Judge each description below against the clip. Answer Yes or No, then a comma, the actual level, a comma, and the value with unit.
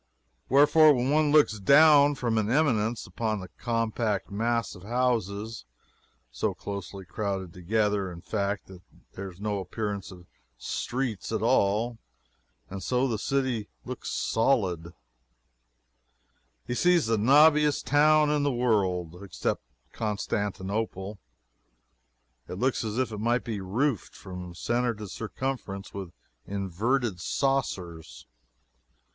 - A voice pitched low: Yes, low, 110 Hz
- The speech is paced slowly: Yes, slow, 125 wpm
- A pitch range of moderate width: Yes, average, 4.7 semitones